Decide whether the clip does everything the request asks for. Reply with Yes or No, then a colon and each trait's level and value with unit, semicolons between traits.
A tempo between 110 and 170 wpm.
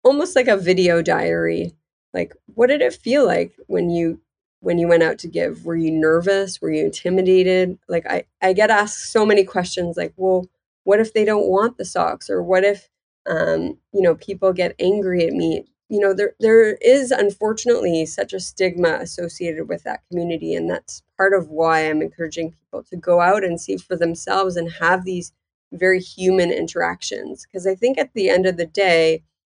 No: average, 195 wpm